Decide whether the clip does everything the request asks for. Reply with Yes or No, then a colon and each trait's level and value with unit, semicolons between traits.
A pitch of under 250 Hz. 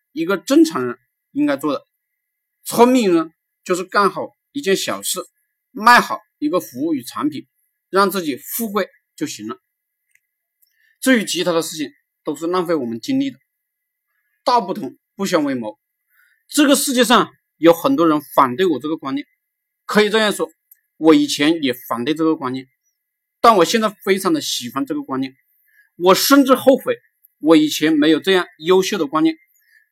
No: very high, 255 Hz